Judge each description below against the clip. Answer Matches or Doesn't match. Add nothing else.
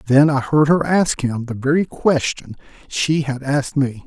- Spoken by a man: Matches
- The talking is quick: Doesn't match